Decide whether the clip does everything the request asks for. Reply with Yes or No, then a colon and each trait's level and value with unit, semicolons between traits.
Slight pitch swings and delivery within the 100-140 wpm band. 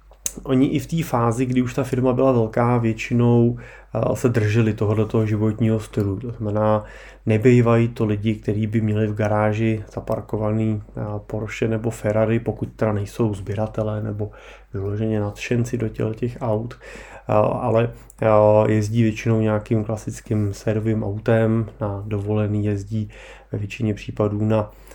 Yes: narrow, 1.7 semitones; average, 130 wpm